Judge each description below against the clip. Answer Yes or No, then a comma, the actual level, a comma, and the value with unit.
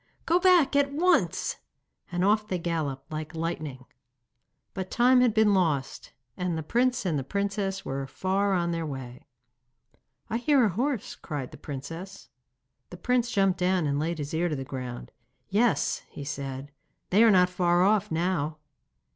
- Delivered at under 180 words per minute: Yes, average, 165 wpm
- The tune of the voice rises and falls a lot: Yes, wide, 5.9 semitones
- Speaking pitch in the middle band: Yes, medium, 180 Hz